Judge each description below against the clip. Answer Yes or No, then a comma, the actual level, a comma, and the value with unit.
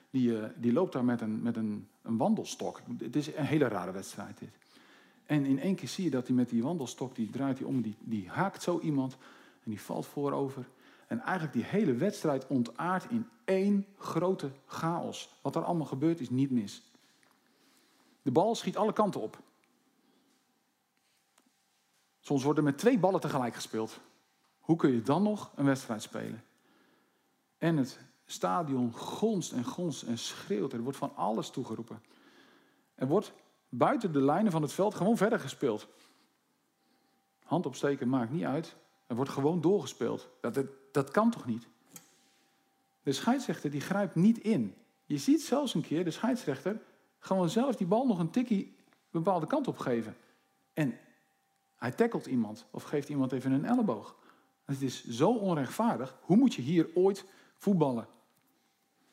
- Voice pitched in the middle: Yes, medium, 155 Hz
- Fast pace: No, average, 165 wpm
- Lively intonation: Yes, wide, 7.7 semitones